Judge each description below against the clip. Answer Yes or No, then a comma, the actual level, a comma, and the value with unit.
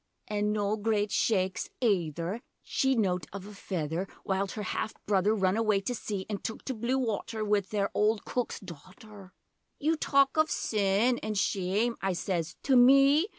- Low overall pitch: No, high, 210 Hz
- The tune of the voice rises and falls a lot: No, average, 3.4 semitones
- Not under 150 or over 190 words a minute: Yes, average, 170 wpm